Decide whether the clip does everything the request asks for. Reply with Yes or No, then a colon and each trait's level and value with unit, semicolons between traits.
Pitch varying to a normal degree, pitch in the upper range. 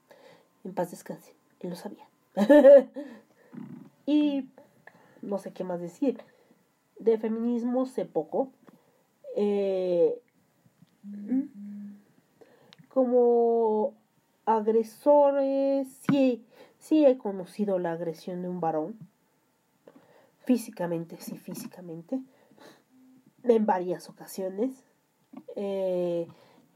No: wide, 6.0 semitones; high, 225 Hz